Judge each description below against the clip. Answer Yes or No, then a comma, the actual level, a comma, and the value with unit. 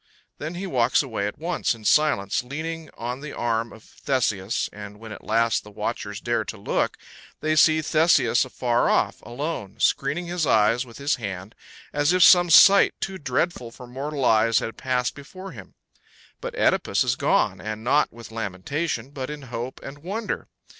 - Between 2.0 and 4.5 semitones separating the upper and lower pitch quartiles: No, wide, 5.5 semitones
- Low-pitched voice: Yes, low, 130 Hz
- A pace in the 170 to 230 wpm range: Yes, average, 175 wpm